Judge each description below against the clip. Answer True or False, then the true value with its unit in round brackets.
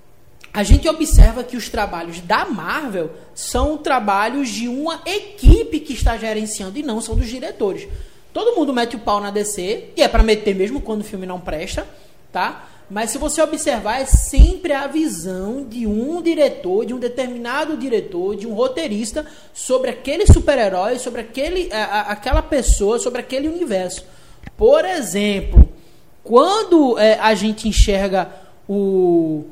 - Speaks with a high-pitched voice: True (245 Hz)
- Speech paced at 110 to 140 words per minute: False (155 wpm)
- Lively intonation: True (6.3 semitones)